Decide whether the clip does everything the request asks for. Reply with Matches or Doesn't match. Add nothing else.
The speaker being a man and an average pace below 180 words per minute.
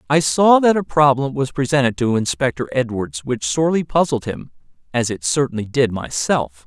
Matches